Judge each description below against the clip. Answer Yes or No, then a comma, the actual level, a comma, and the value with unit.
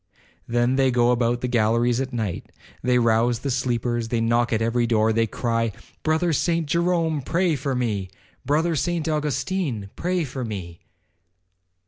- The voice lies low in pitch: Yes, low, 120 Hz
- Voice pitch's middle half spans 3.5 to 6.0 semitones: Yes, average, 4.6 semitones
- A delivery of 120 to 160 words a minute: Yes, average, 145 wpm